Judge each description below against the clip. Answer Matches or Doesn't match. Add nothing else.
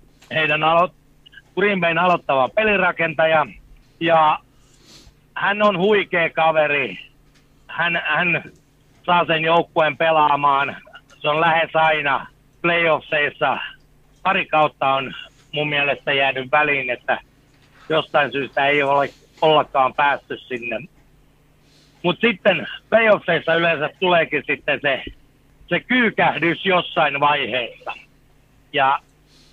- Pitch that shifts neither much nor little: Matches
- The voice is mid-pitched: Matches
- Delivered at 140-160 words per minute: Doesn't match